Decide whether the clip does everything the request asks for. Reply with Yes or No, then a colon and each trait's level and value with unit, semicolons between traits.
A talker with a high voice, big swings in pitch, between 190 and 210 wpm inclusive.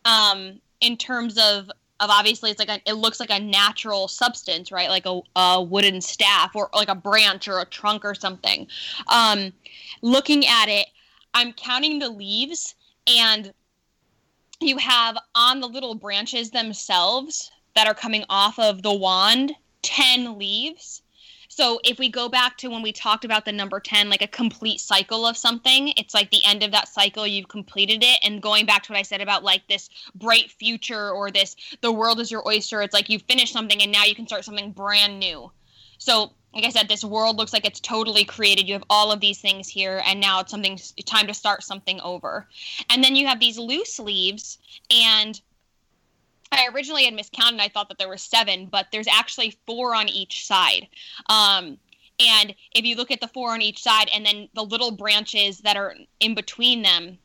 No: high, 215 Hz; average, 2.7 semitones; average, 200 wpm